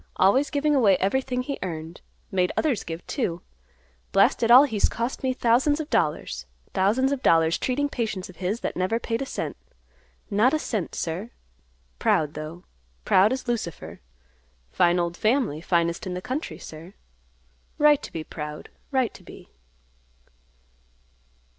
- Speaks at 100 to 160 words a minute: Yes, average, 155 wpm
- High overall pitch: Yes, high, 210 Hz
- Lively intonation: Yes, wide, 7.3 semitones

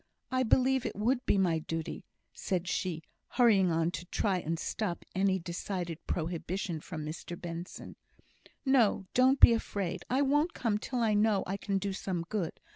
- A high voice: Yes, high, 195 Hz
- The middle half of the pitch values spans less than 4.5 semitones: No, average, 4.8 semitones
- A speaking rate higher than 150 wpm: Yes, average, 170 wpm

